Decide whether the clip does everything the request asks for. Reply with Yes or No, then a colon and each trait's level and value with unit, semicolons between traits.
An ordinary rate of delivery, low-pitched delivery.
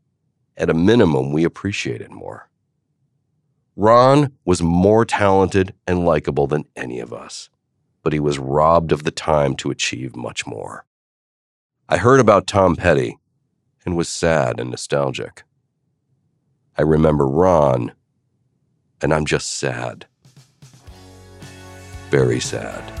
No: slow, 125 wpm; very low, 95 Hz